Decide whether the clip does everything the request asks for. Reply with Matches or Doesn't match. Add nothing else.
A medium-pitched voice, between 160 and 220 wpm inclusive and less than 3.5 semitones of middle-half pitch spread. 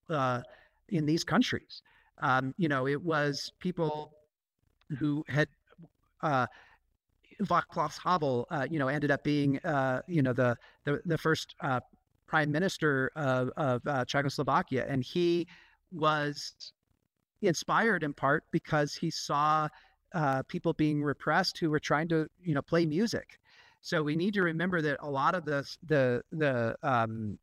Doesn't match